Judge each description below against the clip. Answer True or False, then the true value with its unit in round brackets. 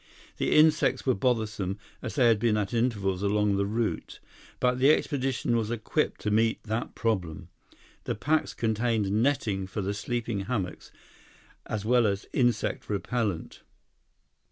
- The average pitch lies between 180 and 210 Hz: False (110 Hz)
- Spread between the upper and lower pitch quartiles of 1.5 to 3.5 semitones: True (3.2 semitones)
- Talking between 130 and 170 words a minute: True (145 wpm)